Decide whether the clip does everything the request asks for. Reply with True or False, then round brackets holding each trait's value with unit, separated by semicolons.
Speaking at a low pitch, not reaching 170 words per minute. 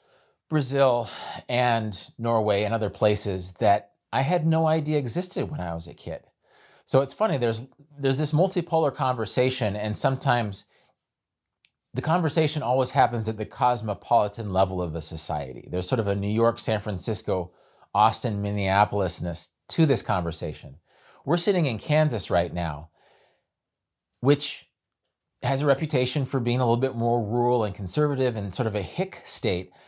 True (120 Hz; 155 wpm)